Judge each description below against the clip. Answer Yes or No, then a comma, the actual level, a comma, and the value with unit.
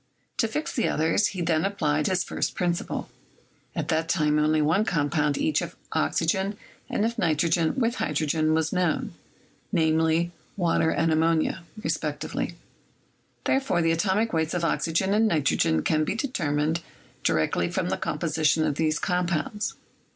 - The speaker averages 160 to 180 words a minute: No, average, 145 wpm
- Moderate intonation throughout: Yes, average, 3.2 semitones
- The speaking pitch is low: No, medium, 165 Hz